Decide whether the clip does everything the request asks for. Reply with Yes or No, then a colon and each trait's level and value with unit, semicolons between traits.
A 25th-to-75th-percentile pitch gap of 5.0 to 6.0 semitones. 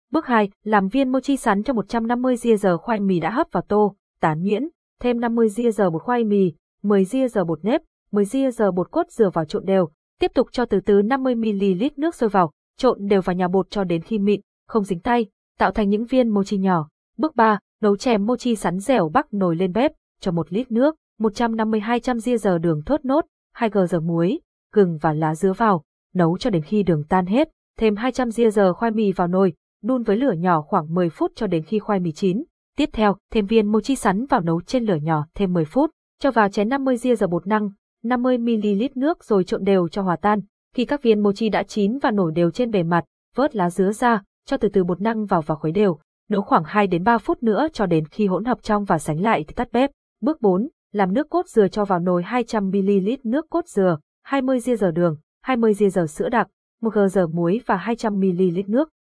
No: average, 4.5 semitones